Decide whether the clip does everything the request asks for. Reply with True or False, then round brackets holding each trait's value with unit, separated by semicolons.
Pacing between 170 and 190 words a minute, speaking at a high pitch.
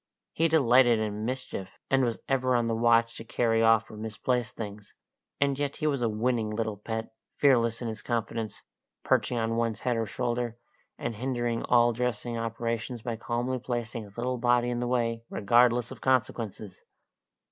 False (175 wpm; 115 Hz)